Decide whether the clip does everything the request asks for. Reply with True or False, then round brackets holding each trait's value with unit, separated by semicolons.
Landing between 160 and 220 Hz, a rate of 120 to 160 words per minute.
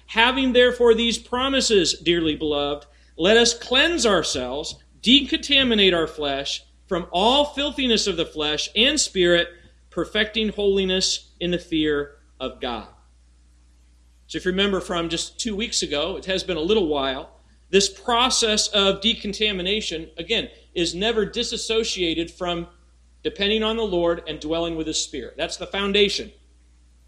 True (190 Hz; 140 wpm)